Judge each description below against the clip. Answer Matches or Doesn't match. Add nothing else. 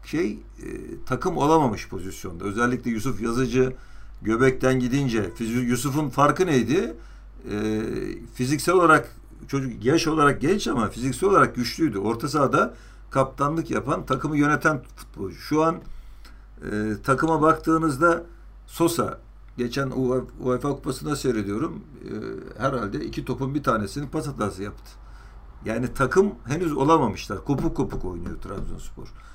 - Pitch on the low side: Matches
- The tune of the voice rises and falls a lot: Doesn't match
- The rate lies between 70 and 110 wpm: Doesn't match